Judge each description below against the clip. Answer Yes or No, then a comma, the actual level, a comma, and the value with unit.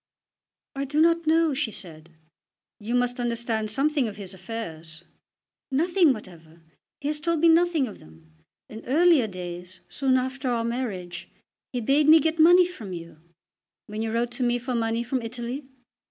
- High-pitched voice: Yes, high, 240 Hz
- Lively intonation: Yes, wide, 6.0 semitones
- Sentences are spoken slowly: No, average, 170 wpm